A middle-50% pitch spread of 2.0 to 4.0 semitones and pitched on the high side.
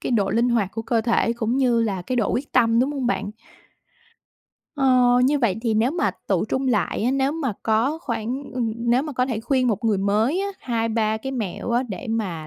Yes: average, 2.9 semitones; high, 235 Hz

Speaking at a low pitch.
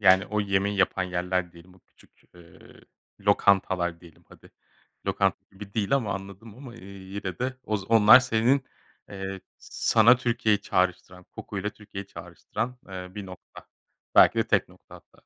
Yes: low, 100 Hz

